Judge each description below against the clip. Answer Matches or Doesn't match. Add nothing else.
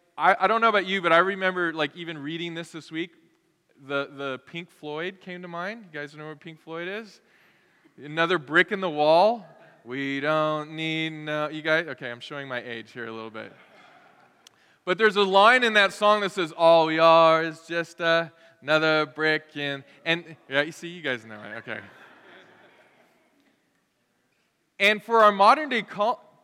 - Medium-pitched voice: Matches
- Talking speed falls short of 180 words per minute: Doesn't match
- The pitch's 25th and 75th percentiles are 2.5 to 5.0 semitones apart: Matches